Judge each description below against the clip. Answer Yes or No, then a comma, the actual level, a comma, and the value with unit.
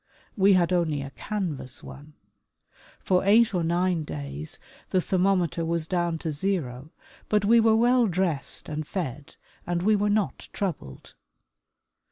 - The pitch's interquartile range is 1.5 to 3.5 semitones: No, average, 4.6 semitones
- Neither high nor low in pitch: Yes, medium, 175 Hz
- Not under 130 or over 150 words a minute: Yes, average, 145 wpm